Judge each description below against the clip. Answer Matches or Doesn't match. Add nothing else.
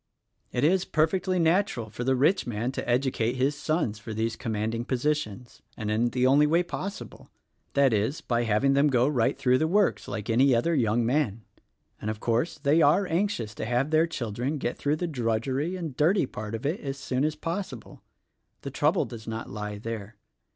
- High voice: Doesn't match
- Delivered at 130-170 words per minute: Doesn't match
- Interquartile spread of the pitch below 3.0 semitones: Doesn't match